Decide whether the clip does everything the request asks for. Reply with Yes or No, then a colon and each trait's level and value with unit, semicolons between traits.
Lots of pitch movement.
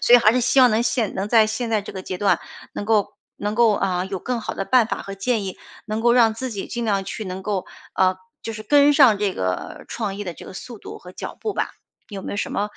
No: average, 3.3 semitones